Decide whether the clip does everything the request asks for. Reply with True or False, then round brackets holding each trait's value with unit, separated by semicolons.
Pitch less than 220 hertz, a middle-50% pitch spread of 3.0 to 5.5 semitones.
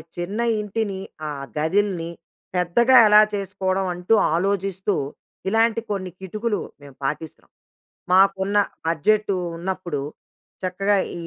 False (190 Hz; 2.5 semitones)